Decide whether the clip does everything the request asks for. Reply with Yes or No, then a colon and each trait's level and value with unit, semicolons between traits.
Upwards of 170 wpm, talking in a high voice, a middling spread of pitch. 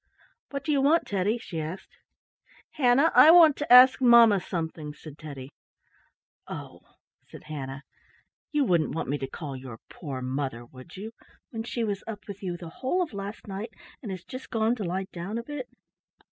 No: average, 185 wpm; high, 195 Hz; wide, 7.9 semitones